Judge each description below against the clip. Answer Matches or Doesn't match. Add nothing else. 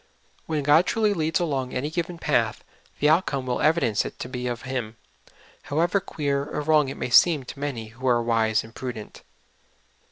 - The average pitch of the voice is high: Doesn't match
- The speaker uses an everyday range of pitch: Matches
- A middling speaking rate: Doesn't match